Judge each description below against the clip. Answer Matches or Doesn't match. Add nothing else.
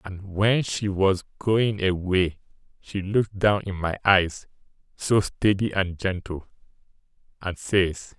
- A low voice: Matches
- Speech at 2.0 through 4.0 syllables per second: Matches